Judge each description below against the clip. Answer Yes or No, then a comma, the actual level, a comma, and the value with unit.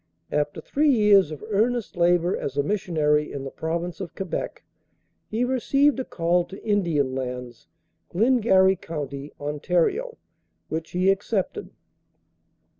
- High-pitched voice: No, medium, 180 Hz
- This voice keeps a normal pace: No, slow, 125 wpm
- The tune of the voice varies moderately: No, wide, 6.0 semitones